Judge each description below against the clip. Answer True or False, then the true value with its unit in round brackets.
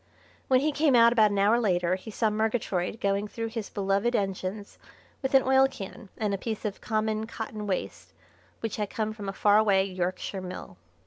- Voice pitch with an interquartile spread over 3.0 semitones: False (2.5 semitones)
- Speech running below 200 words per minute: True (190 wpm)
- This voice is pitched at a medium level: False (210 Hz)